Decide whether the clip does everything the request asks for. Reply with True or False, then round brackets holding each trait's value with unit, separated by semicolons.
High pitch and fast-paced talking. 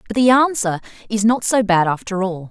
True (215 Hz; 215 wpm)